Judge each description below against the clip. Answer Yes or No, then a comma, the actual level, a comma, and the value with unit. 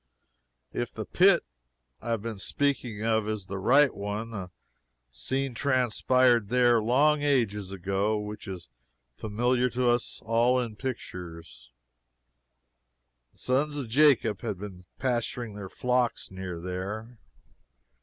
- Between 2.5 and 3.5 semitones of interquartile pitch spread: No, average, 4.0 semitones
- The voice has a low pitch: Yes, low, 115 Hz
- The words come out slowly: Yes, slow, 125 wpm